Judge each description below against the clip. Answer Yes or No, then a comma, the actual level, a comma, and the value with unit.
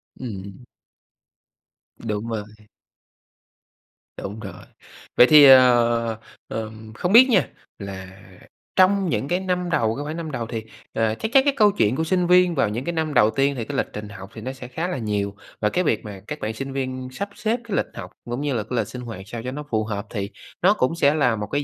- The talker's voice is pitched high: No, low, 125 Hz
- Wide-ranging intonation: Yes, wide, 6.6 semitones